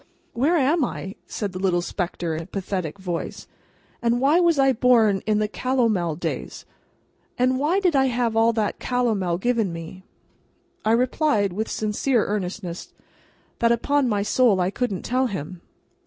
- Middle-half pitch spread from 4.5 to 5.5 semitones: Yes, average, 5.2 semitones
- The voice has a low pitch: No, high, 220 Hz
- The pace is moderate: Yes, average, 160 wpm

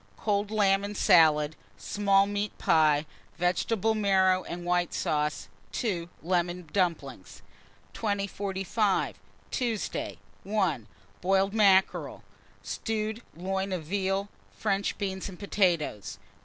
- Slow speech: Yes, slow, 105 wpm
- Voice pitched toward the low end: No, high, 190 Hz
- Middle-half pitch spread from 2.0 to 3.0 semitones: Yes, average, 2.7 semitones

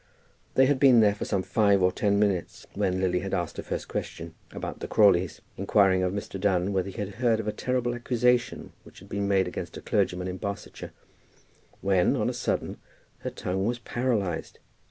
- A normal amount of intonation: Yes, average, 3.1 semitones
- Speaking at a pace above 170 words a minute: Yes, average, 195 wpm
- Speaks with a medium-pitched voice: No, low, 100 Hz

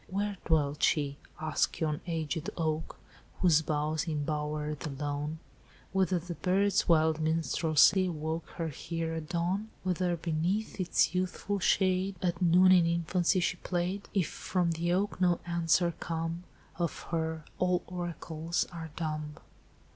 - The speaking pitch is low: No, medium, 170 Hz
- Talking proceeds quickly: No, average, 140 wpm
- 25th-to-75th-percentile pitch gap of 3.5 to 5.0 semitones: No, narrow, 2.5 semitones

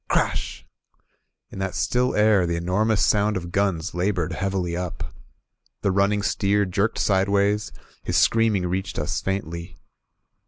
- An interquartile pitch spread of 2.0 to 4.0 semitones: Yes, narrow, 2.5 semitones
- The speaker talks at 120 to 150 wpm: Yes, average, 140 wpm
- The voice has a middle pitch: No, low, 100 Hz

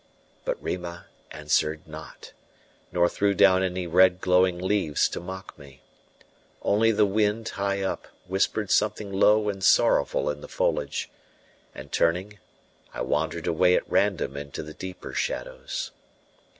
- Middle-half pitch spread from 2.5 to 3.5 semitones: Yes, average, 3.2 semitones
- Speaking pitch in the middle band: No, very low, 95 Hz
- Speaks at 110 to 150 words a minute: Yes, slow, 135 wpm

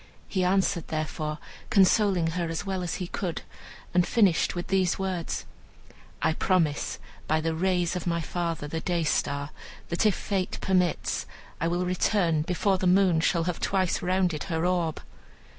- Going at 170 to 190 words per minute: No, average, 160 wpm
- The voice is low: No, medium, 175 Hz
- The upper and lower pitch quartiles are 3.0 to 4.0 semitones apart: No, narrow, 2.4 semitones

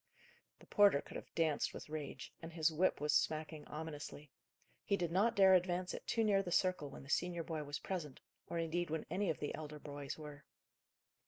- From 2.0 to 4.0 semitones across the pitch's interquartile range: Yes, average, 3.4 semitones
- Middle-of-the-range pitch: Yes, medium, 160 Hz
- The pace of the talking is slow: No, average, 200 wpm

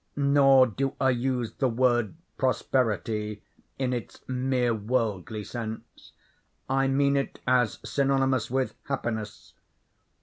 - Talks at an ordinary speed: No, slow, 110 wpm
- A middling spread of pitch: Yes, average, 3.0 semitones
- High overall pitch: No, low, 125 Hz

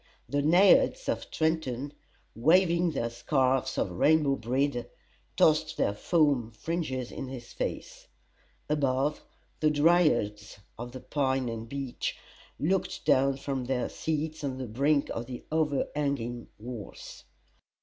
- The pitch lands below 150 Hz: Yes, medium, 140 Hz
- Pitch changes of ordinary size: Yes, average, 4.1 semitones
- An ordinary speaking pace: No, slow, 125 wpm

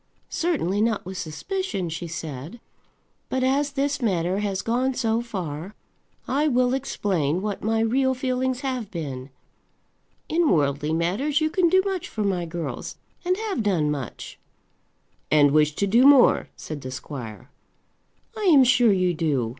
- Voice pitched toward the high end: Yes, high, 210 Hz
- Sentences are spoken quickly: No, average, 155 wpm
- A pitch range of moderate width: No, wide, 8.6 semitones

